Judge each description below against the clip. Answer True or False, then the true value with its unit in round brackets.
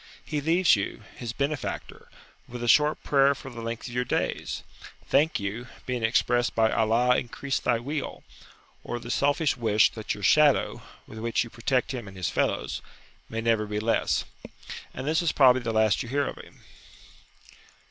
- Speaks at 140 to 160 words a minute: False (180 wpm)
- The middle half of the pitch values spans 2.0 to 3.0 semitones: False (3.7 semitones)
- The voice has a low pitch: True (120 Hz)